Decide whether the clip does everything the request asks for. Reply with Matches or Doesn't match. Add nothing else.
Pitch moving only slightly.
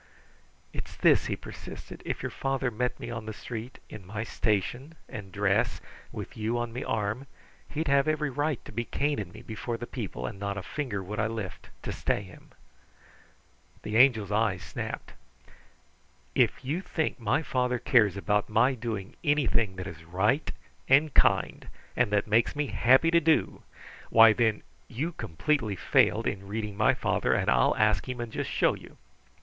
Doesn't match